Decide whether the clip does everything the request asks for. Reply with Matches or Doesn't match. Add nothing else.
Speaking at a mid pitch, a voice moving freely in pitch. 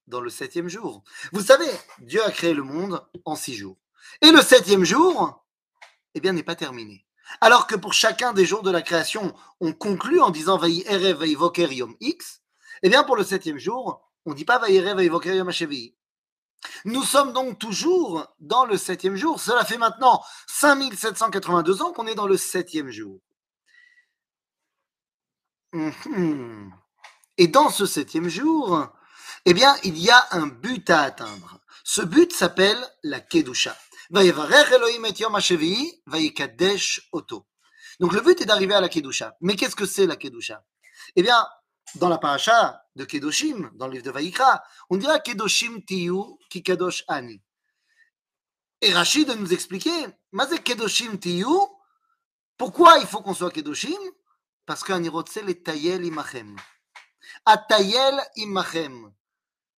Doesn't match